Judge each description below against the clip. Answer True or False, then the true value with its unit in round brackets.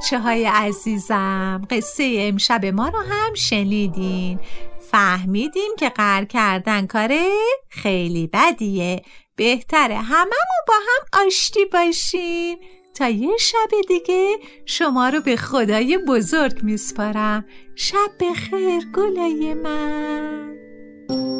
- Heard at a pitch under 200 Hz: False (250 Hz)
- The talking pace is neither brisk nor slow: False (100 wpm)